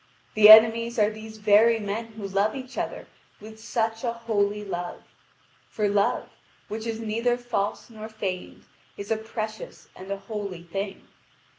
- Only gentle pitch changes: Yes, narrow, 1.9 semitones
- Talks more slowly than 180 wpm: Yes, average, 155 wpm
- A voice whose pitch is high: Yes, high, 215 Hz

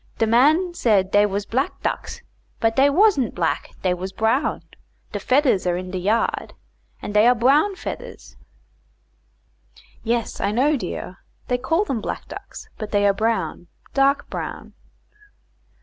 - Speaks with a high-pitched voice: Yes, high, 225 Hz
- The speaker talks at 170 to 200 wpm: No, average, 150 wpm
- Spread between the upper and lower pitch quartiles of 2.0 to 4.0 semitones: No, wide, 5.4 semitones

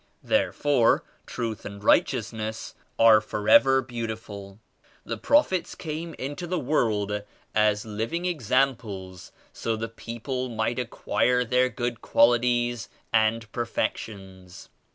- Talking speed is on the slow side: Yes, slow, 115 wpm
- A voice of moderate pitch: No, low, 115 Hz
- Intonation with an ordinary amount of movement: Yes, average, 3.0 semitones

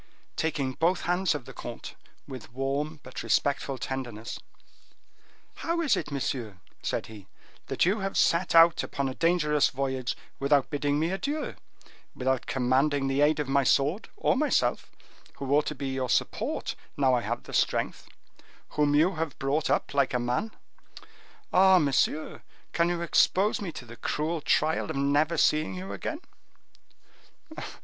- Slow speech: No, average, 155 wpm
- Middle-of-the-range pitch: Yes, medium, 145 Hz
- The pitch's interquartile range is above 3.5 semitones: Yes, average, 4.0 semitones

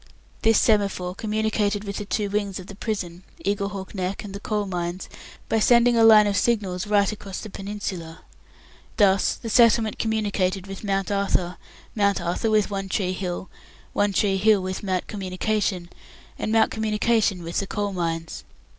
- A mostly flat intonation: Yes, narrow, 2.3 semitones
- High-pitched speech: Yes, high, 200 Hz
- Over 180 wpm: No, average, 165 wpm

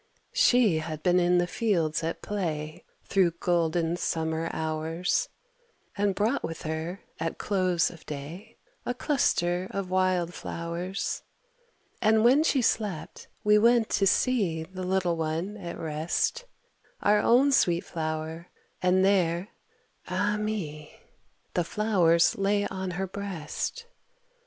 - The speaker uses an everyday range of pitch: Yes, average, 3.9 semitones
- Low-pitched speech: No, medium, 180 Hz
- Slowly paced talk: Yes, slow, 130 wpm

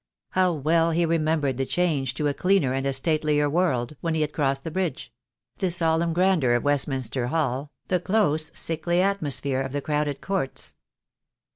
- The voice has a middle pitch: Yes, medium, 150 Hz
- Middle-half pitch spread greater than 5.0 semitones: No, average, 3.9 semitones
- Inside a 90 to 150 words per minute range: No, average, 175 wpm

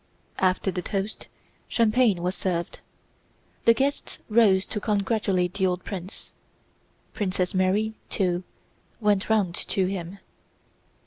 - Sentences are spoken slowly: Yes, slow, 115 wpm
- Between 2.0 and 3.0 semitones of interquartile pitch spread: Yes, average, 2.7 semitones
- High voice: Yes, high, 195 Hz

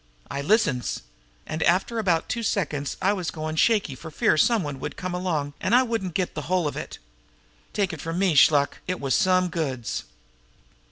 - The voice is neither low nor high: Yes, medium, 170 Hz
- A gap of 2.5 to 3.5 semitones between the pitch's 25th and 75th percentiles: No, average, 4.4 semitones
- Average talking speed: Yes, average, 190 wpm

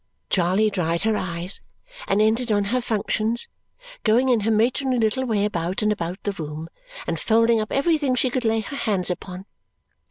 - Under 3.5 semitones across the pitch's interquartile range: No, average, 4.1 semitones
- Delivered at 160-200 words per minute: Yes, average, 180 wpm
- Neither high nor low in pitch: No, high, 215 Hz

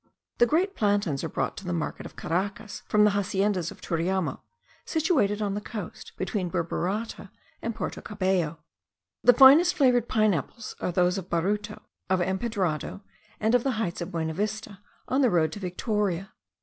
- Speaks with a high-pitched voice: Yes, high, 200 Hz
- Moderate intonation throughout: Yes, average, 3.6 semitones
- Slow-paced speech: No, average, 165 wpm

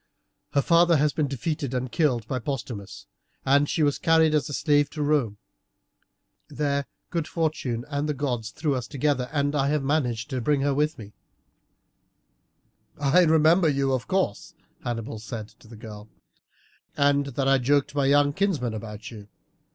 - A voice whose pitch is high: No, medium, 140 Hz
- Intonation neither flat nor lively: Yes, average, 3.6 semitones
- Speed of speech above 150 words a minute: Yes, average, 165 wpm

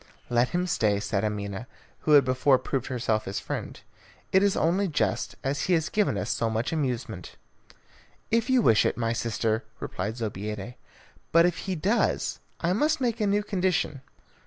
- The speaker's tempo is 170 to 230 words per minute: Yes, average, 175 wpm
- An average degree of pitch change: No, wide, 8.8 semitones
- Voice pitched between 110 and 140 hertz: Yes, low, 135 Hz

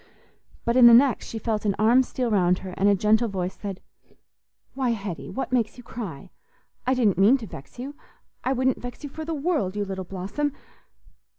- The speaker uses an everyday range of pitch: Yes, average, 4.7 semitones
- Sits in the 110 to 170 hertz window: No, high, 225 Hz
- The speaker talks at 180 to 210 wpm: Yes, average, 200 wpm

